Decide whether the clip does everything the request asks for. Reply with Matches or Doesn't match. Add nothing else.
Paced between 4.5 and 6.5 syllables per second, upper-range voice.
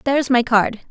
Matches